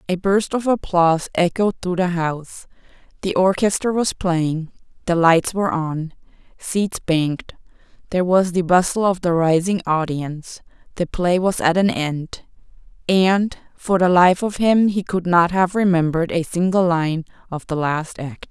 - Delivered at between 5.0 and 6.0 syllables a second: No, 4.5 syllables/s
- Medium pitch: Yes, medium, 180 Hz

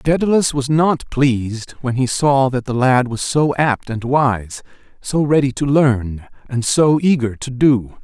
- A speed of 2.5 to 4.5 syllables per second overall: Yes, 4.1 syllables/s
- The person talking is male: Yes, male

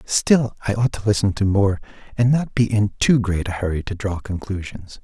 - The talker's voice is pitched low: Yes, low, 105 Hz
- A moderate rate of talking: No, fast, 215 wpm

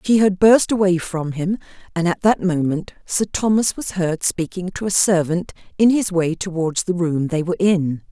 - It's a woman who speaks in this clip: Yes, female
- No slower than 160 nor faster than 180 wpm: No, average, 200 wpm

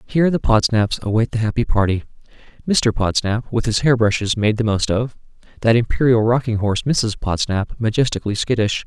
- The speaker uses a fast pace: No, average, 170 wpm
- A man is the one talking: Yes, male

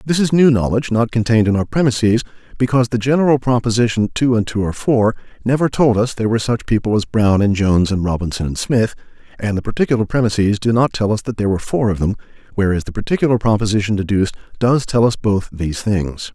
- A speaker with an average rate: No, fast, 215 wpm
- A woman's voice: No, male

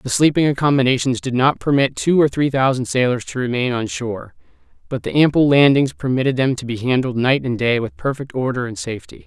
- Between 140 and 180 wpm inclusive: No, fast, 205 wpm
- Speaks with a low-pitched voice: Yes, low, 130 Hz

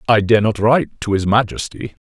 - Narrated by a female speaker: No, male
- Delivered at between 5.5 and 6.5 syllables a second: Yes, 5.6 syllables/s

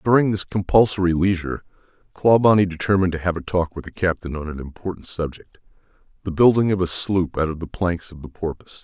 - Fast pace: No, average, 190 wpm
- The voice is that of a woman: No, male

